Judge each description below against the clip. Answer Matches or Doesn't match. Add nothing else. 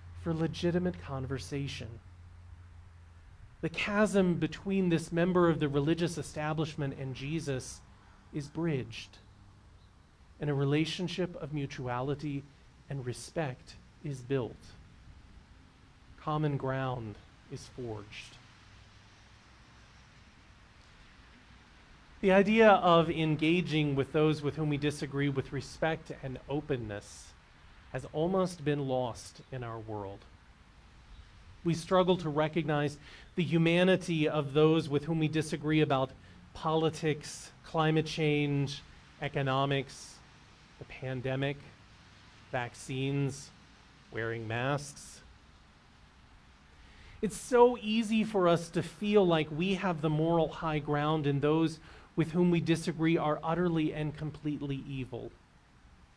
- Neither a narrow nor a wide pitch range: Doesn't match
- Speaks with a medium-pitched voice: Matches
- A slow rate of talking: Matches